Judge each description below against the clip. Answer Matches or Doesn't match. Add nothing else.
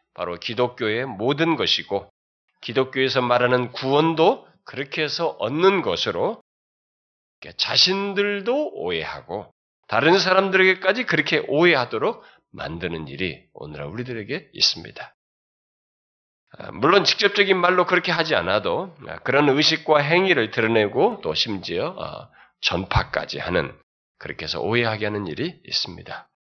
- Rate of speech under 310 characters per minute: Matches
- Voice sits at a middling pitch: Matches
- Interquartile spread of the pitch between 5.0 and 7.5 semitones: Doesn't match